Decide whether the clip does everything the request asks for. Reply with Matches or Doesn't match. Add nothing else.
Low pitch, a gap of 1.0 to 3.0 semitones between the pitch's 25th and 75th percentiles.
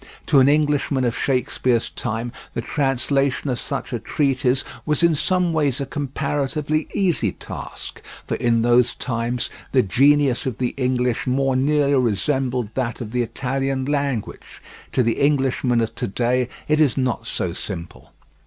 Matches